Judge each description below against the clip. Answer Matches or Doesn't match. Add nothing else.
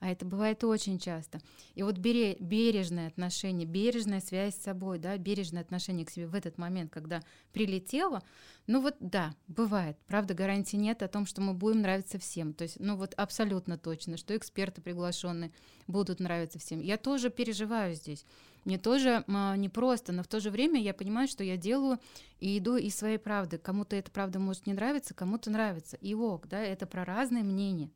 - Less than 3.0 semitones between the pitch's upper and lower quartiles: Doesn't match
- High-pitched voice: Matches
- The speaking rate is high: Matches